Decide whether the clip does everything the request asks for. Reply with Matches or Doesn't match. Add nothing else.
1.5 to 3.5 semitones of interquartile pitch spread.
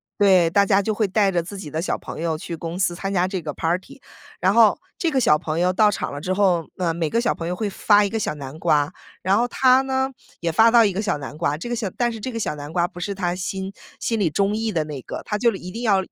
Doesn't match